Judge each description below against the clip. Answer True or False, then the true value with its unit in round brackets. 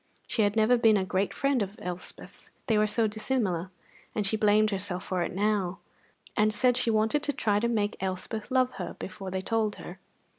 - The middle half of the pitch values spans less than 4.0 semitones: True (2.8 semitones)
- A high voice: True (210 Hz)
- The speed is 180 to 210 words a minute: True (200 wpm)